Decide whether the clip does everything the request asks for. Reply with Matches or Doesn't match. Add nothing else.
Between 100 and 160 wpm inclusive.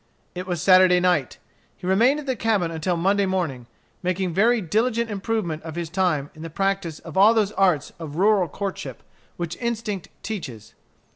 Doesn't match